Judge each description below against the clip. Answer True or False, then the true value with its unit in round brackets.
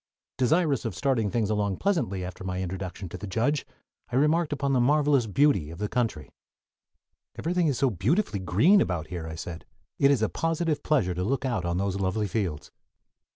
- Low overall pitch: True (110 Hz)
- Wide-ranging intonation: True (7.7 semitones)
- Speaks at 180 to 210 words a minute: True (185 wpm)